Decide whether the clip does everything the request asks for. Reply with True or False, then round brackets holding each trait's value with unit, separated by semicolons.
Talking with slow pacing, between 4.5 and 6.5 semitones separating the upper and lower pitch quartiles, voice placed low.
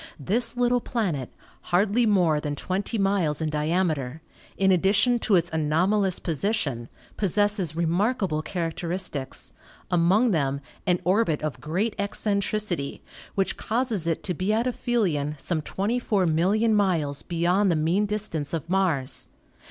False (130 wpm; 4.8 semitones; 185 Hz)